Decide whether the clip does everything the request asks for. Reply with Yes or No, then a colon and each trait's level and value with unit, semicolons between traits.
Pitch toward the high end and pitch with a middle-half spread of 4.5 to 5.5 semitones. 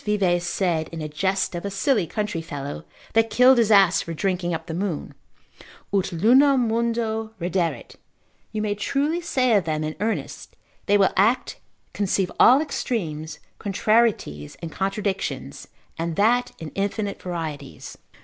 Yes: high, 195 Hz; average, 4.9 semitones